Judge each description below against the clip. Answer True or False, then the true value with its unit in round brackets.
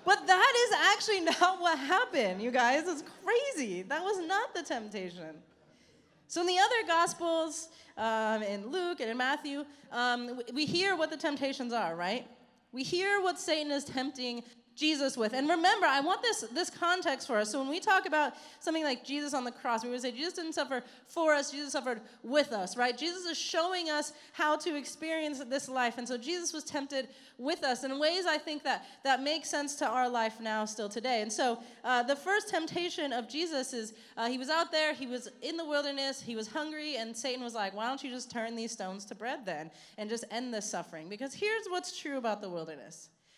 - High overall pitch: True (275 Hz)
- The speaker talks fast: True (215 wpm)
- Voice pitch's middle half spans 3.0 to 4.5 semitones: False (5.3 semitones)